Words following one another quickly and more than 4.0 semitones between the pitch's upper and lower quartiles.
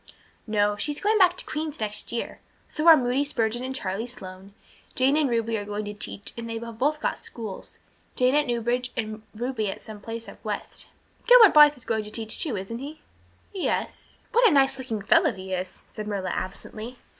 Yes: fast, 210 wpm; average, 5.1 semitones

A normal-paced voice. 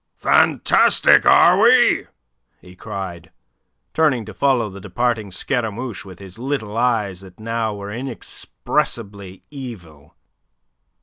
No: slow, 110 wpm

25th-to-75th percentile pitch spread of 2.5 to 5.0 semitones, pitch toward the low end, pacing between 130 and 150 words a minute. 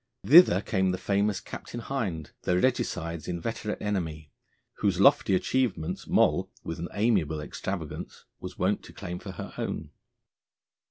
Yes: average, 4.1 semitones; very low, 95 Hz; average, 140 wpm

